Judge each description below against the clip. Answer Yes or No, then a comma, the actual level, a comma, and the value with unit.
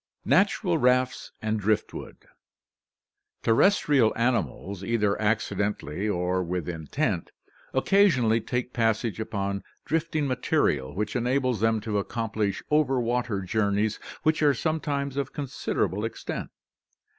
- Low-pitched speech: Yes, low, 115 Hz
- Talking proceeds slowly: Yes, slow, 115 wpm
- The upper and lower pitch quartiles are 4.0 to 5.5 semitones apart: Yes, average, 4.6 semitones